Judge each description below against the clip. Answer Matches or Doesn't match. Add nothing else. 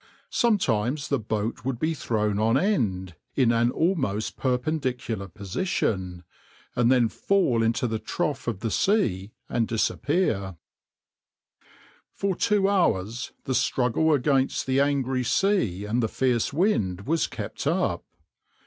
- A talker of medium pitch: Doesn't match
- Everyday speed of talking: Doesn't match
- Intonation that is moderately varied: Doesn't match